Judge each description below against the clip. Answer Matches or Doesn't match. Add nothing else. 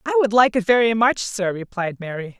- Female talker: Matches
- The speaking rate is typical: Doesn't match